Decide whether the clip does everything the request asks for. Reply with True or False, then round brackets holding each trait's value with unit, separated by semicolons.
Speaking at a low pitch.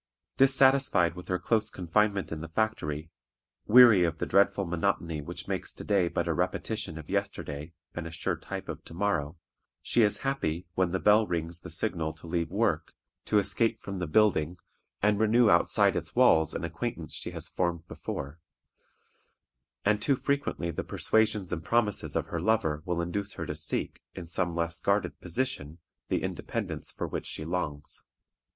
True (90 Hz)